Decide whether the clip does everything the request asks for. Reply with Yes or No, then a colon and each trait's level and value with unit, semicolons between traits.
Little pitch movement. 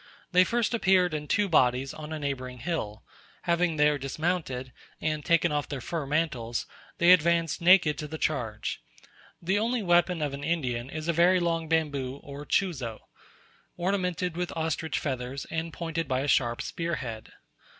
No: average, 4.0 semitones